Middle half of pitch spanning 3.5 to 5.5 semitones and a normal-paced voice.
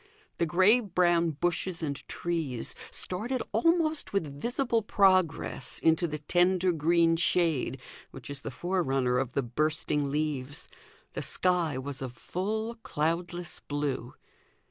No: average, 4.4 semitones; slow, 125 wpm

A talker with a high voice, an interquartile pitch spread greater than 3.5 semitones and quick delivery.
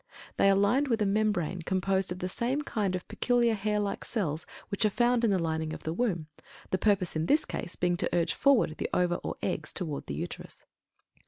Yes: high, 195 Hz; average, 4.0 semitones; fast, 220 wpm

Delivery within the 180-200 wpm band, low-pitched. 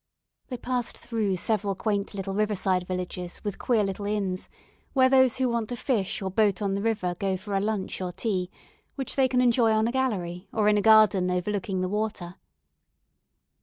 No: average, 190 wpm; high, 205 Hz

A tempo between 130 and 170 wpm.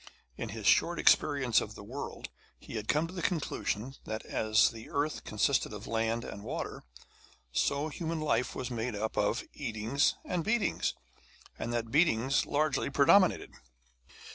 Yes: average, 160 wpm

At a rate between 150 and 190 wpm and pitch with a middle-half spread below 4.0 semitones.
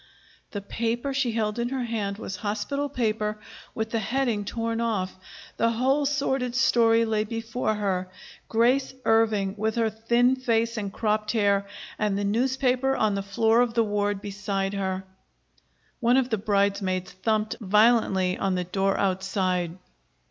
Yes: average, 155 wpm; average, 3.0 semitones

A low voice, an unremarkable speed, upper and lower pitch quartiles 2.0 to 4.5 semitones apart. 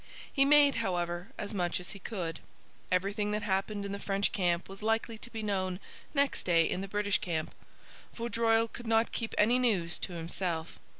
No: high, 200 Hz; average, 185 wpm; average, 3.9 semitones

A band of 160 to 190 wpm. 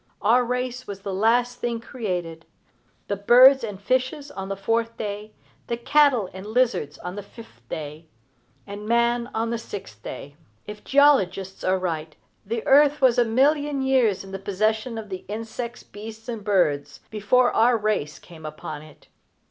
Yes: average, 170 wpm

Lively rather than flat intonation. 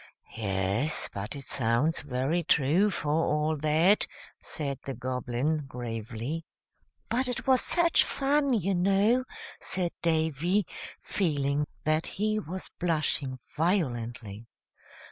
Yes: wide, 6.4 semitones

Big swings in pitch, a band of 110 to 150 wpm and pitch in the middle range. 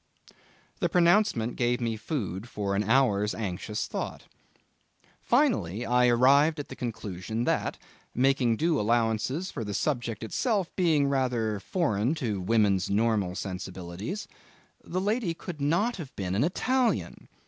No: wide, 7.0 semitones; slow, 135 wpm; low, 120 Hz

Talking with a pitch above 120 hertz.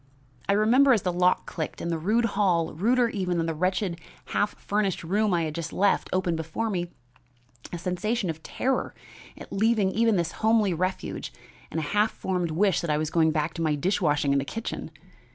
Yes: medium, 185 Hz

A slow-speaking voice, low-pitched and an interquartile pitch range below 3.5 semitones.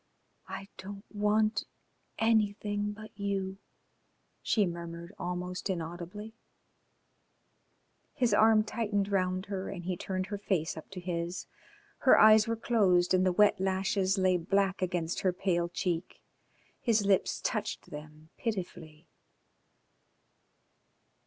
No: slow, 120 wpm; high, 190 Hz; average, 2.7 semitones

